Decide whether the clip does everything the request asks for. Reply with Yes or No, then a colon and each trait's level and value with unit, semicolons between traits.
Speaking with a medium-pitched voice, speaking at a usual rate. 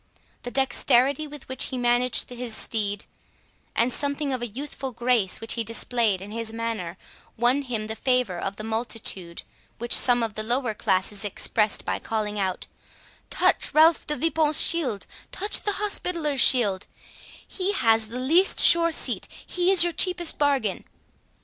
No: high, 245 Hz; average, 155 wpm